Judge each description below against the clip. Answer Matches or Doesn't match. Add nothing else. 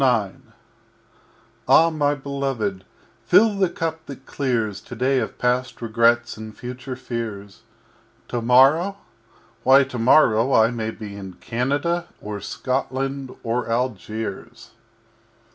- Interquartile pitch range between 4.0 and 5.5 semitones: Doesn't match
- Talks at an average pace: Doesn't match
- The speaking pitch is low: Matches